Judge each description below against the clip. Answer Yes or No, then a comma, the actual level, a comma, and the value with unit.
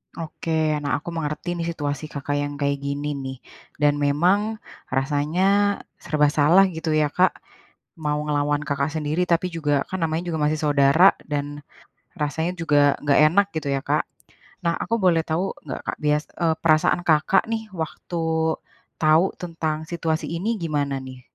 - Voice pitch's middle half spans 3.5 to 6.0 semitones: No, average, 2.8 semitones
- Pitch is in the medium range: Yes, medium, 155 Hz